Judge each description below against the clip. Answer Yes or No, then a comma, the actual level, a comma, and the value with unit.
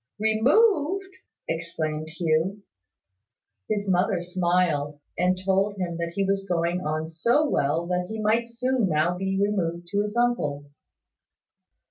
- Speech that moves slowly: Yes, slow, 130 wpm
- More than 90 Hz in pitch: Yes, medium, 185 Hz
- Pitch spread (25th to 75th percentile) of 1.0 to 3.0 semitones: No, average, 4.3 semitones